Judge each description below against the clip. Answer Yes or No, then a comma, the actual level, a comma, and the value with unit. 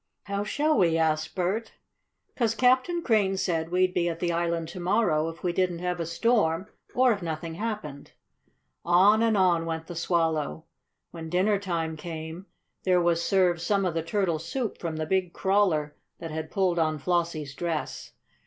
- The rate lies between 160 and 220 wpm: Yes, average, 175 wpm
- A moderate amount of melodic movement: Yes, average, 3.3 semitones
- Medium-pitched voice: Yes, medium, 175 Hz